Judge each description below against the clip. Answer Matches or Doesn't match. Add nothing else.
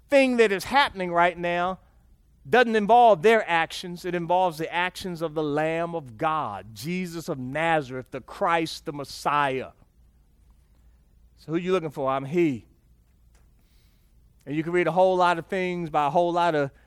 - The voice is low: Doesn't match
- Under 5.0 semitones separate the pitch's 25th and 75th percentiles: Doesn't match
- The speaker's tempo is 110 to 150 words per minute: Doesn't match